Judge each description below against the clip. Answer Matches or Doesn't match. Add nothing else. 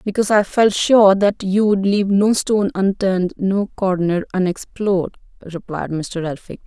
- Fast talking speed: Doesn't match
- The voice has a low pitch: Doesn't match